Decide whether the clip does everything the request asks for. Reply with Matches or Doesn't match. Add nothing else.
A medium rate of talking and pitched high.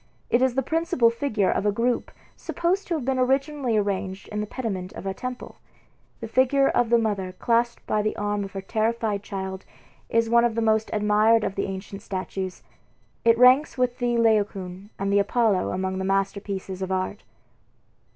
Matches